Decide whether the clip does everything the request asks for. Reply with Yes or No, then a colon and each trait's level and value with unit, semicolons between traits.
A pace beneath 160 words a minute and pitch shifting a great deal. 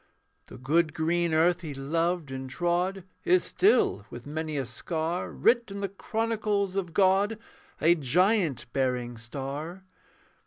Yes: average, 140 wpm; wide, 5.8 semitones